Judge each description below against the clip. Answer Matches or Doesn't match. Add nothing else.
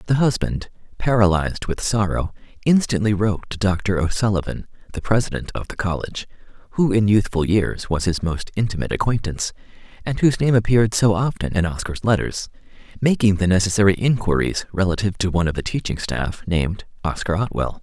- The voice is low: Matches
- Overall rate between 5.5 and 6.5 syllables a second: Matches